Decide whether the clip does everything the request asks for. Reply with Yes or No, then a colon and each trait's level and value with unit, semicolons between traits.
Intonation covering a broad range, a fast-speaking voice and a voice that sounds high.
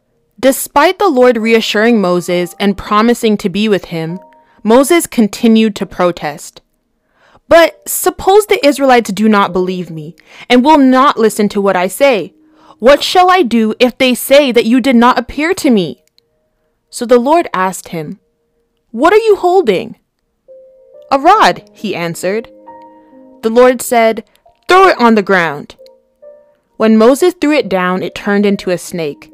No: wide, 7.4 semitones; average, 155 wpm; high, 230 Hz